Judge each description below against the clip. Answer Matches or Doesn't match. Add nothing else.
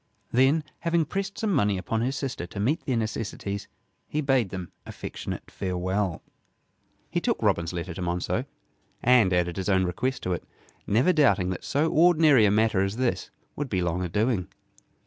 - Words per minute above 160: Matches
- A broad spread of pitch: Matches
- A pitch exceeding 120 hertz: Doesn't match